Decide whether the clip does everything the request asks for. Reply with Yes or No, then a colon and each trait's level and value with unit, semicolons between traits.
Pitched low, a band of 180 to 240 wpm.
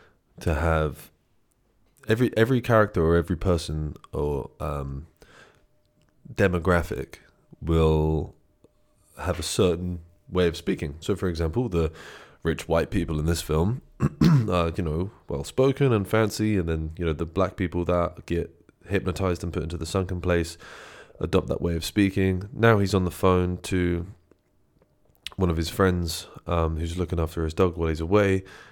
No: very low, 90 Hz; average, 155 wpm